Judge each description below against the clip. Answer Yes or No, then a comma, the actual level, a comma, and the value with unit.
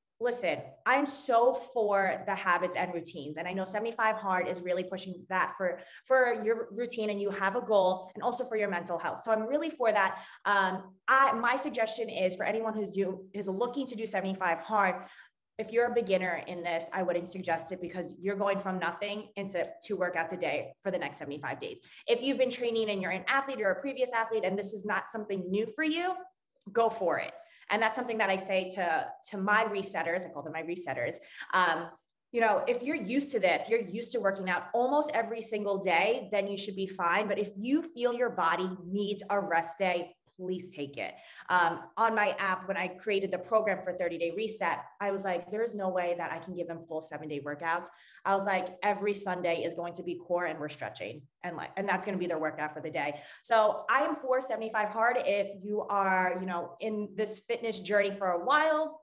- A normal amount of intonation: Yes, average, 4.0 semitones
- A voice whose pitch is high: Yes, high, 200 Hz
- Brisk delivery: Yes, fast, 225 wpm